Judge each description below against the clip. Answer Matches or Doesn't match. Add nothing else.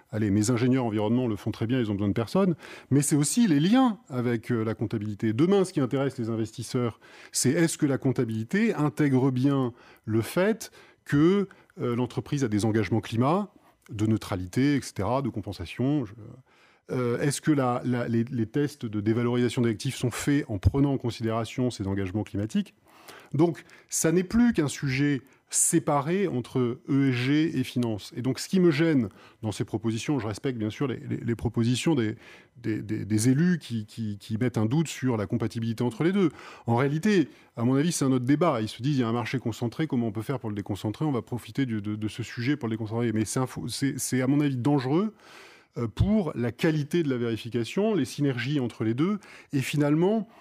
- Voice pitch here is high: Doesn't match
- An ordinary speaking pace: Matches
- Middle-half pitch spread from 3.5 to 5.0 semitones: Matches